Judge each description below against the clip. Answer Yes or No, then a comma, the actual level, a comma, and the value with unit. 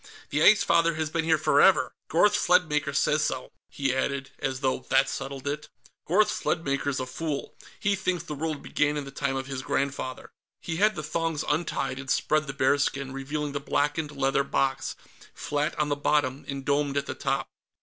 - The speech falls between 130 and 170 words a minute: No, average, 190 wpm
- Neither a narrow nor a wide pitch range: No, narrow, 2.3 semitones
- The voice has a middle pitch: Yes, medium, 145 Hz